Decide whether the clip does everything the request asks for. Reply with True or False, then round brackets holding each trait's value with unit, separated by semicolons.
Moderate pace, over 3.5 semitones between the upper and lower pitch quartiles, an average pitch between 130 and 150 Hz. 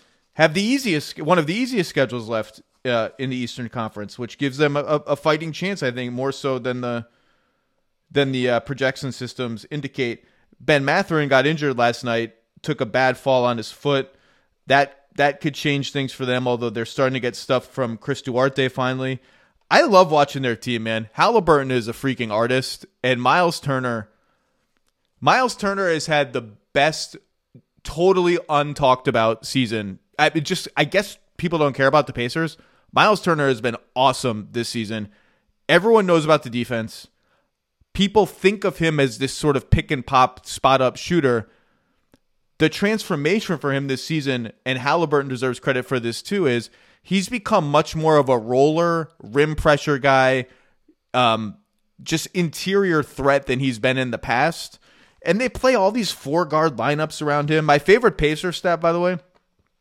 True (175 wpm; 4.4 semitones; 140 Hz)